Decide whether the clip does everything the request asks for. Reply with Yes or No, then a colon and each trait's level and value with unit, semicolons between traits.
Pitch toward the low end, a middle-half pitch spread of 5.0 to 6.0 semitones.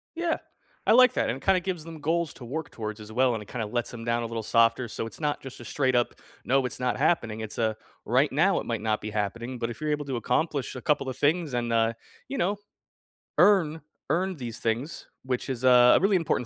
Yes: low, 125 Hz; average, 5.3 semitones